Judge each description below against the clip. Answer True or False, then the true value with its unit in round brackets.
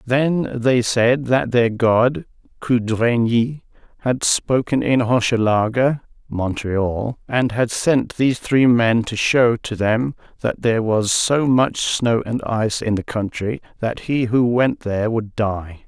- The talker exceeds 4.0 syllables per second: False (3.8 syllables/s)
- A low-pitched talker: True (120 Hz)